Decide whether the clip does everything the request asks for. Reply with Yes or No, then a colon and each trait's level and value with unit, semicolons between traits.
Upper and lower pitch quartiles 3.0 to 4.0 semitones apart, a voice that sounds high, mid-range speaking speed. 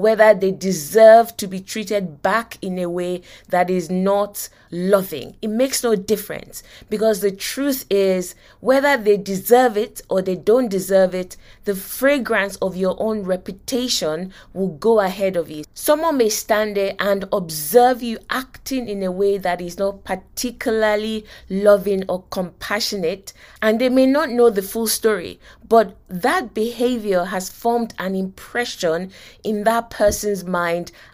Yes: average, 3.3 semitones; high, 205 Hz; average, 150 wpm